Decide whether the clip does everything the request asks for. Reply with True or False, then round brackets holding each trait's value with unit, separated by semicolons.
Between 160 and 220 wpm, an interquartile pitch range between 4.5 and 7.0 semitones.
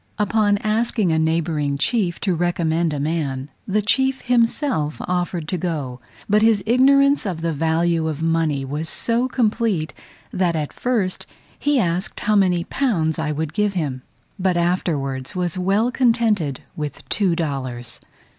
False (150 wpm; 5.2 semitones)